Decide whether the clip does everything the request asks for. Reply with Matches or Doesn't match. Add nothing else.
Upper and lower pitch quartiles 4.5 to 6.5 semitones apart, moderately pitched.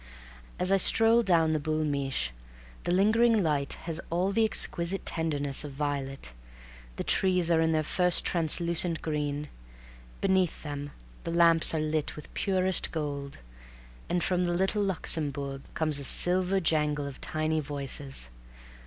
Doesn't match